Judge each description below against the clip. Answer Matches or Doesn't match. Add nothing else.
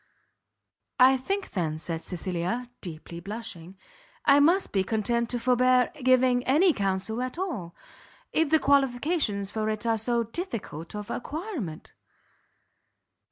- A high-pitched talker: Matches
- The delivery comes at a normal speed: Doesn't match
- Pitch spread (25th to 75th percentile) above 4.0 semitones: Matches